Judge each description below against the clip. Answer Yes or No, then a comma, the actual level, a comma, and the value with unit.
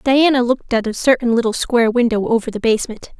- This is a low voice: No, high, 235 Hz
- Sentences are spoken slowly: No, fast, 205 wpm